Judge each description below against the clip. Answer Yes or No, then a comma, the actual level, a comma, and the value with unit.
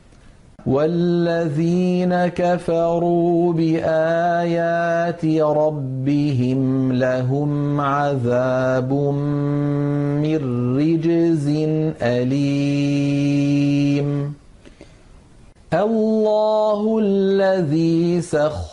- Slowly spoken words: Yes, slow, 40 wpm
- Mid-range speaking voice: Yes, medium, 155 Hz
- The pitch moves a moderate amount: Yes, average, 3.1 semitones